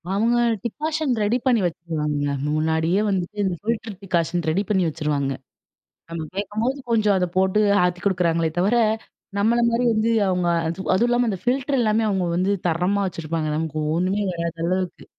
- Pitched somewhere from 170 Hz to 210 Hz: Yes, high, 190 Hz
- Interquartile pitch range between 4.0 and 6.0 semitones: Yes, average, 4.6 semitones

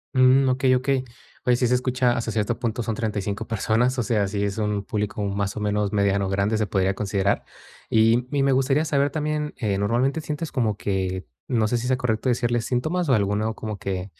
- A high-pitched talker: No, low, 115 Hz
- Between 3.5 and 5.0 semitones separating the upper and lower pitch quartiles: Yes, average, 4.0 semitones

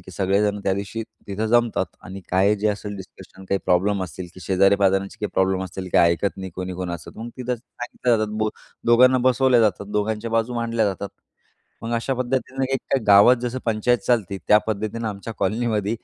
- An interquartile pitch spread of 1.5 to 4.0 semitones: Yes, average, 3.2 semitones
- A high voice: No, low, 105 Hz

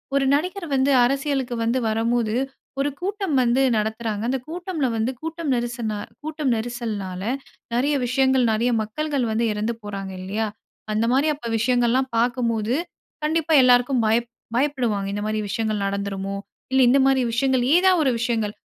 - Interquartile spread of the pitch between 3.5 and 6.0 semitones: Yes, average, 4.0 semitones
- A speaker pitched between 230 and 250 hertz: Yes, high, 245 Hz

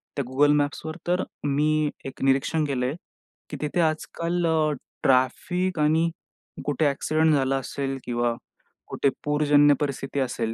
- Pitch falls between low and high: Yes, medium, 145 Hz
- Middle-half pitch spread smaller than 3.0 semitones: Yes, narrow, 2.6 semitones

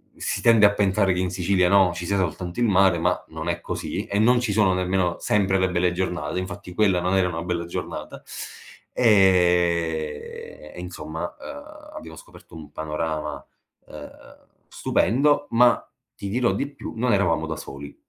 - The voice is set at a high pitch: No, very low, 90 Hz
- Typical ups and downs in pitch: Yes, average, 3.1 semitones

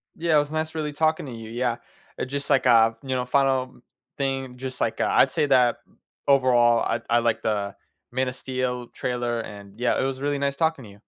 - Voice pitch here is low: Yes, low, 130 Hz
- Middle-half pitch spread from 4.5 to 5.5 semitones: No, average, 2.8 semitones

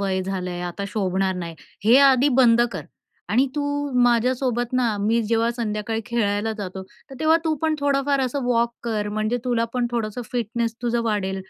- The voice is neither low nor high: No, high, 230 Hz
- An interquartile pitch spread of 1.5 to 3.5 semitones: Yes, average, 3.2 semitones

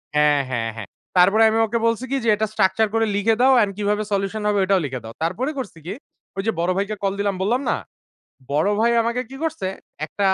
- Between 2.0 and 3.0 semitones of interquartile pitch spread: No, average, 3.4 semitones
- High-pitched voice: Yes, high, 205 Hz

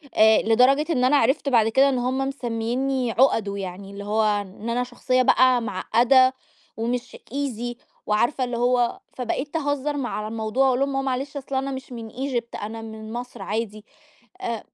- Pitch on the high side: Yes, high, 245 Hz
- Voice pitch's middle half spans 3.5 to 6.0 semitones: No, average, 3.1 semitones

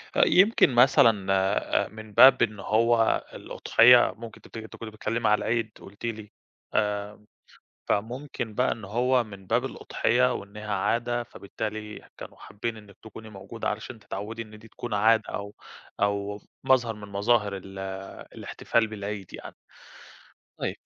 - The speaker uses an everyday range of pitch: No, narrow, 2.3 semitones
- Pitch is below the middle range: Yes, low, 110 Hz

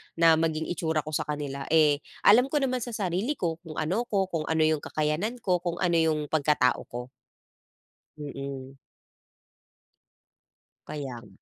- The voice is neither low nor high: Yes, medium, 160 Hz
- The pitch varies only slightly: No, average, 3.4 semitones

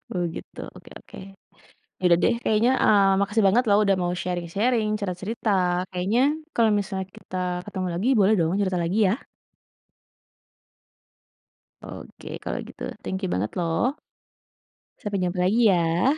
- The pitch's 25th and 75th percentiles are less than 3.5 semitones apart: Yes, average, 3.1 semitones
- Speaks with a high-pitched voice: Yes, high, 195 Hz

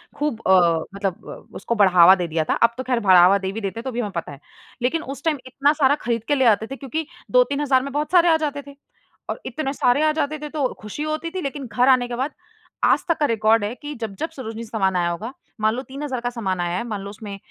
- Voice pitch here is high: Yes, high, 245 Hz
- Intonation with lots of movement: Yes, wide, 5.9 semitones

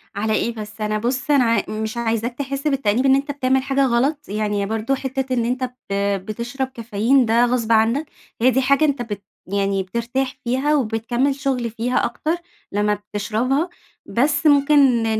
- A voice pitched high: Yes, high, 245 Hz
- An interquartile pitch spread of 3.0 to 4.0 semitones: Yes, average, 3.7 semitones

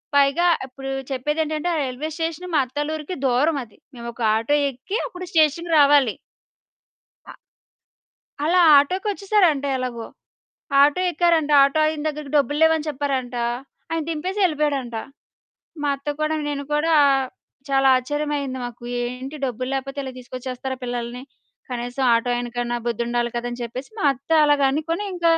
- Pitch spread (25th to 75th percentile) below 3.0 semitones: No, average, 3.8 semitones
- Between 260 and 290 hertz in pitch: Yes, very high, 280 Hz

